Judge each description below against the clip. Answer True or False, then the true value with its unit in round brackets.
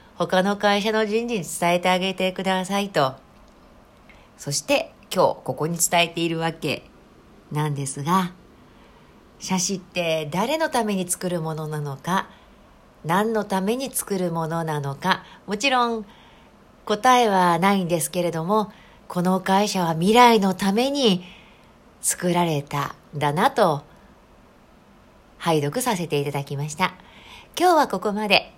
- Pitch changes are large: False (4.5 semitones)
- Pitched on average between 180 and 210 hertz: True (185 Hz)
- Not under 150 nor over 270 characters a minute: True (255 characters per minute)